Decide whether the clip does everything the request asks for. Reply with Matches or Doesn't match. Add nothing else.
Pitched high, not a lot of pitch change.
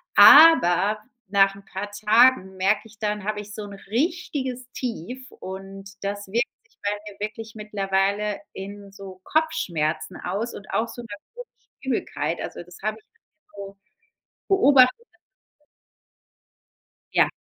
Doesn't match